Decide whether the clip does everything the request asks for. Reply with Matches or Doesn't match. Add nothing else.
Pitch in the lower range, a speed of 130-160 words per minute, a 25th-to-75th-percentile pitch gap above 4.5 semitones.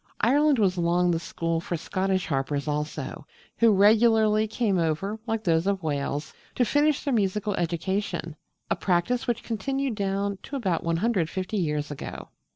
Doesn't match